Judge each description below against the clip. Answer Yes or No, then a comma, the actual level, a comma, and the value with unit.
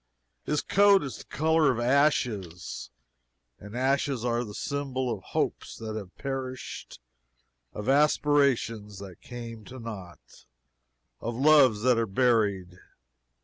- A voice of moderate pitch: No, low, 120 Hz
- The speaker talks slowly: Yes, slow, 125 wpm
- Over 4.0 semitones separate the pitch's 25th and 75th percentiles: Yes, average, 4.8 semitones